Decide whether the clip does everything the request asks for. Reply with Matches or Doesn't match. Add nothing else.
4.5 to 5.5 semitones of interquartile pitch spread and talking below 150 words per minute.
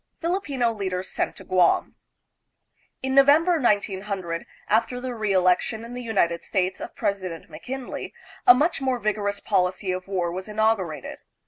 Matches